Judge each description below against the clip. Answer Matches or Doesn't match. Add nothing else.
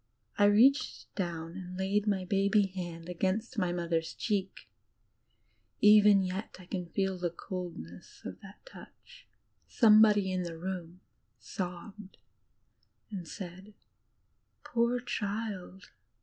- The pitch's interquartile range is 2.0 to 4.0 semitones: Matches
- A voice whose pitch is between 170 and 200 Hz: Matches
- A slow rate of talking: Matches